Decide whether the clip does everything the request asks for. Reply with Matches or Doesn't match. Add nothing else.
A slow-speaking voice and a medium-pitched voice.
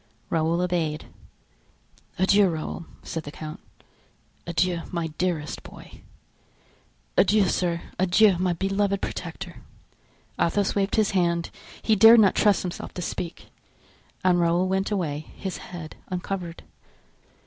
Matches